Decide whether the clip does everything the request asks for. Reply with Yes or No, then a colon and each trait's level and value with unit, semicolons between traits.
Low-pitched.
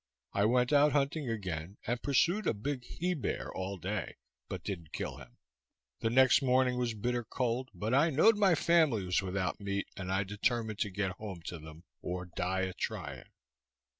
Yes: low, 110 Hz